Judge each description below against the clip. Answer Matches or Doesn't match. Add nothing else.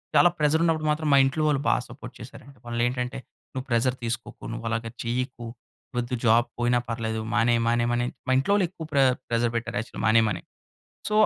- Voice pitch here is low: Matches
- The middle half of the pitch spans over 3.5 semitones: Doesn't match